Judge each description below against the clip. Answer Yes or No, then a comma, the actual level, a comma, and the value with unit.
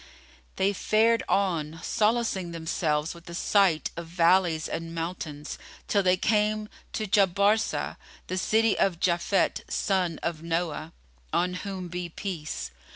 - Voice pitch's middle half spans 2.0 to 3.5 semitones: Yes, average, 3.2 semitones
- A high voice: No, medium, 180 Hz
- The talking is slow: Yes, slow, 130 wpm